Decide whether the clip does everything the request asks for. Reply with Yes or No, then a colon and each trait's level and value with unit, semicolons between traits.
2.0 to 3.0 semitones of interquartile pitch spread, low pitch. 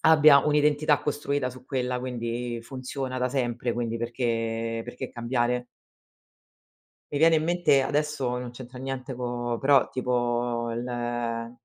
Yes: narrow, 2.4 semitones; low, 125 Hz